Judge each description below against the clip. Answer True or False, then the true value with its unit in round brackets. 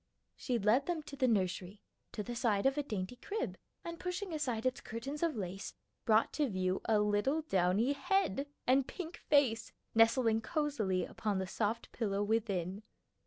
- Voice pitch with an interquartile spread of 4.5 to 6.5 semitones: True (5.6 semitones)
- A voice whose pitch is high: True (230 Hz)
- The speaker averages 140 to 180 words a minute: True (165 wpm)